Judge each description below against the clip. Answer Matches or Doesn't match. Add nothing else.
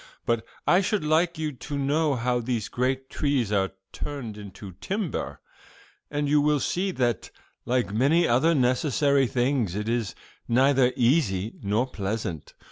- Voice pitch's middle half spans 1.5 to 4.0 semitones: Doesn't match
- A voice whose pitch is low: Matches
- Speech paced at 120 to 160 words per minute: Matches